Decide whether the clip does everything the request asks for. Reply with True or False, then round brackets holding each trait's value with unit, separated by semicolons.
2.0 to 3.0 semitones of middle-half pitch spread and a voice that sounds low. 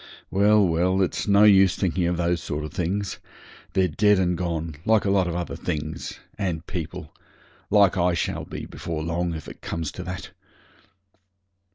True (2.7 semitones; 90 Hz)